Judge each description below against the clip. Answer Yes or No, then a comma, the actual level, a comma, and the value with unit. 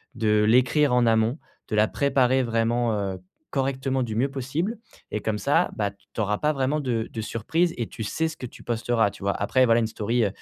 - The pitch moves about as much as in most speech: Yes, average, 3.6 semitones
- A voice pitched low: Yes, low, 120 Hz